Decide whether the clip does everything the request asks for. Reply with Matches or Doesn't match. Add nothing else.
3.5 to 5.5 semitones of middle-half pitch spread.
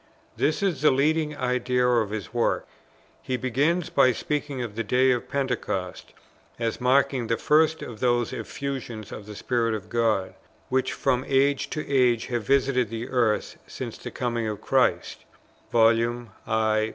Doesn't match